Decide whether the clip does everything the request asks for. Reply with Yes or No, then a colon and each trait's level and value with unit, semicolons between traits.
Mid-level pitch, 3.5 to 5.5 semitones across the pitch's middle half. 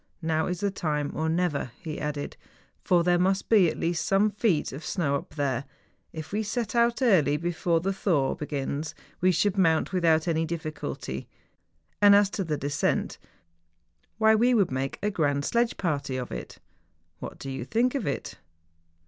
Yes: medium, 165 Hz; average, 5.1 semitones